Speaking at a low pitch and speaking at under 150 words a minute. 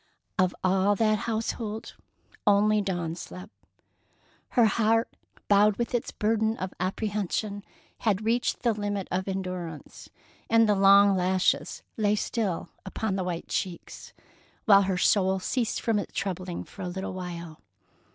No: high, 200 Hz; average, 140 wpm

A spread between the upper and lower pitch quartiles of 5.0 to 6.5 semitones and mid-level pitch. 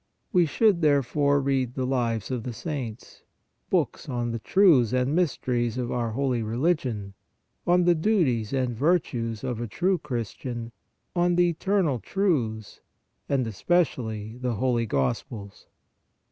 No: wide, 5.5 semitones; low, 125 Hz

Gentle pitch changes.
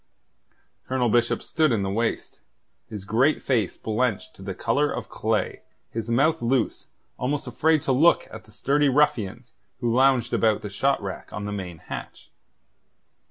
No: average, 4.3 semitones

